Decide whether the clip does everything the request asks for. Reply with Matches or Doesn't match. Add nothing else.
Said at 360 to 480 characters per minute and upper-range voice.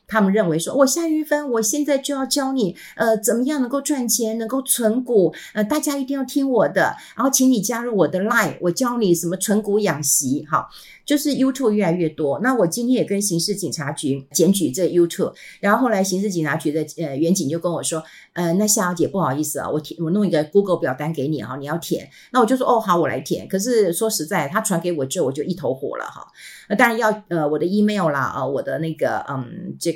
Matches